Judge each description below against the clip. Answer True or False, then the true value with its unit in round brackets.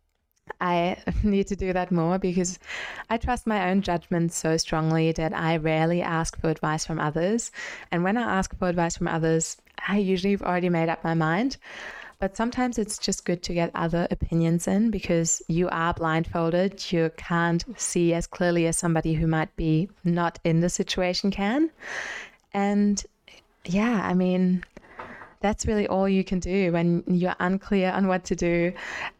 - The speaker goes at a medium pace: True (175 wpm)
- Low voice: False (180 Hz)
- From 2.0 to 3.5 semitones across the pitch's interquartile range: True (2.9 semitones)